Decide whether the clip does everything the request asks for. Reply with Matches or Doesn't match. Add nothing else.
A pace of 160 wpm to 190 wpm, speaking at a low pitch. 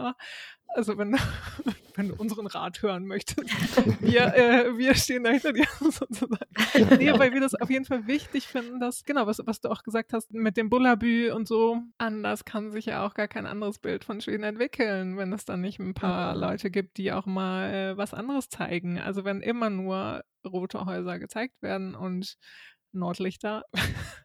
Doesn't match